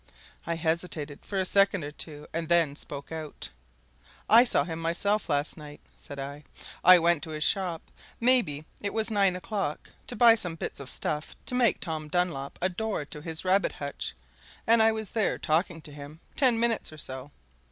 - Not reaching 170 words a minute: No, average, 190 wpm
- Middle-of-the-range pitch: Yes, medium, 170 Hz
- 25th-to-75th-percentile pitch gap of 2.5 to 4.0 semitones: No, average, 5.2 semitones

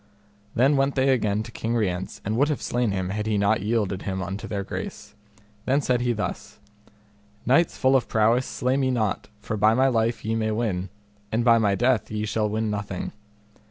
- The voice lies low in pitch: Yes, low, 110 Hz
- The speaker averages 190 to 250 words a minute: Yes, average, 200 wpm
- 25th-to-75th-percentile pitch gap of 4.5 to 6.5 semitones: No, average, 3.0 semitones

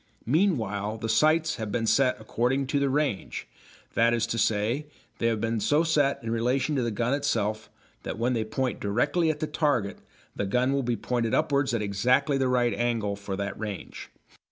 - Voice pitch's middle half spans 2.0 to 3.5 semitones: No, average, 4.1 semitones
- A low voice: Yes, low, 120 Hz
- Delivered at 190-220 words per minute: Yes, average, 195 wpm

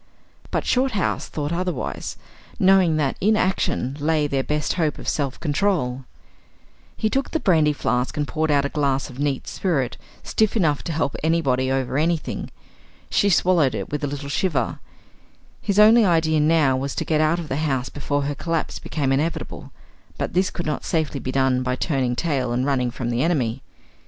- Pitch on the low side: No, medium, 150 Hz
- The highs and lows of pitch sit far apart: No, average, 4.0 semitones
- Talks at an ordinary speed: Yes, average, 180 wpm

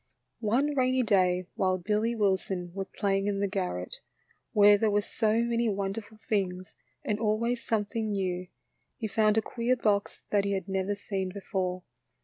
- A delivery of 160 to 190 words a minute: Yes, average, 165 wpm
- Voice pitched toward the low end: No, high, 205 Hz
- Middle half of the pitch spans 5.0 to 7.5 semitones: No, narrow, 2.5 semitones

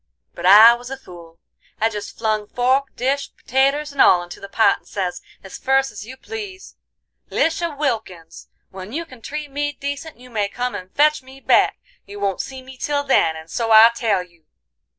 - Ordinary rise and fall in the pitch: No, wide, 5.7 semitones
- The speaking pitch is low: No, high, 245 Hz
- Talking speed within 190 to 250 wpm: Yes, average, 195 wpm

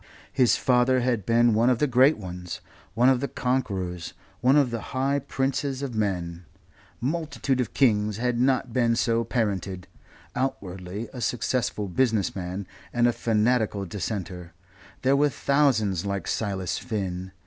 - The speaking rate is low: No, average, 150 wpm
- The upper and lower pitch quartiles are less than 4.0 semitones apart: No, average, 4.9 semitones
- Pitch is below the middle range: Yes, low, 115 Hz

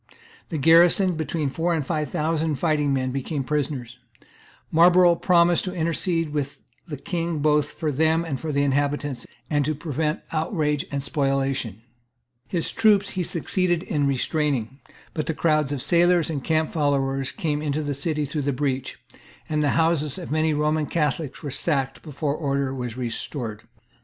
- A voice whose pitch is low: No, medium, 150 Hz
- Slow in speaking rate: No, average, 160 wpm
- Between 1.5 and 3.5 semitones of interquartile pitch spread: Yes, average, 2.8 semitones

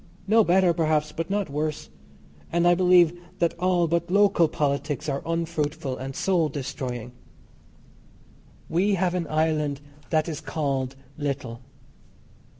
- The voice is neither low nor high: Yes, medium, 160 Hz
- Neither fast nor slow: No, slow, 130 wpm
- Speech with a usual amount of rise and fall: Yes, average, 3.5 semitones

